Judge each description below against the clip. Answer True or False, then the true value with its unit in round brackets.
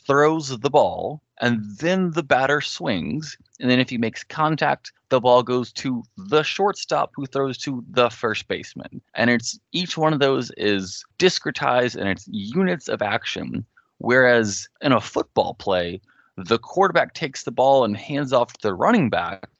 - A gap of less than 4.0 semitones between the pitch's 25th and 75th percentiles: False (4.6 semitones)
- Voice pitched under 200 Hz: True (135 Hz)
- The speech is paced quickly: False (170 wpm)